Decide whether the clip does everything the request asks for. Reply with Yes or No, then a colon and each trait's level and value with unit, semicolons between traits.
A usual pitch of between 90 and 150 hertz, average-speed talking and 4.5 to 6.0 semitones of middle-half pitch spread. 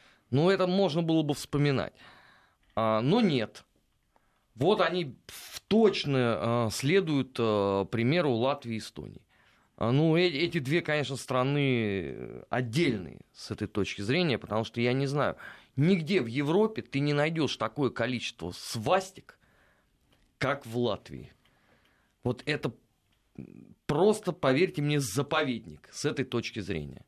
Yes: low, 135 Hz; average, 130 wpm; average, 5.3 semitones